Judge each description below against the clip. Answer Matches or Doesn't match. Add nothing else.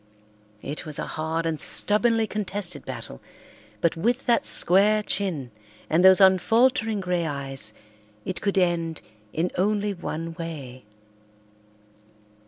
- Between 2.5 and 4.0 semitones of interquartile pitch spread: Doesn't match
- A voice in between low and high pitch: Matches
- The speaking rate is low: Matches